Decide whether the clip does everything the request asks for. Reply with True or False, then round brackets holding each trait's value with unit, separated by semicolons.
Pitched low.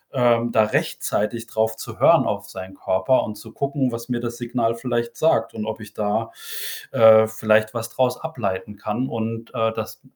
True (115 Hz)